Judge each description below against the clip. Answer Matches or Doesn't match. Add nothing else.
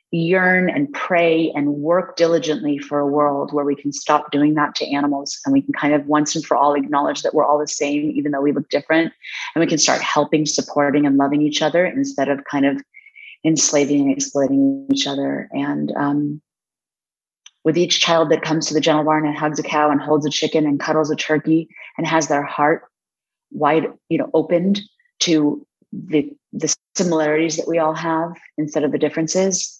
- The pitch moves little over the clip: Matches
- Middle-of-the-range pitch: Matches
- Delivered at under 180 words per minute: Doesn't match